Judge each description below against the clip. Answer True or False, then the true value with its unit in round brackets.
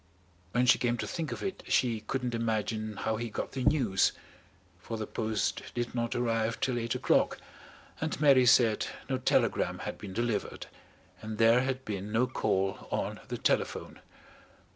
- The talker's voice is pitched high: False (115 Hz)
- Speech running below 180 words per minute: True (165 wpm)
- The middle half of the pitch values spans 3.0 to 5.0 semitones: False (2.5 semitones)